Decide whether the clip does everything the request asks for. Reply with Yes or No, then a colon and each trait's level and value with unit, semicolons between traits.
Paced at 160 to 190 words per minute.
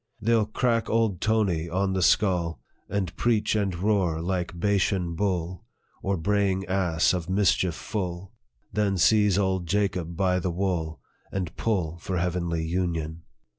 No: average, 145 wpm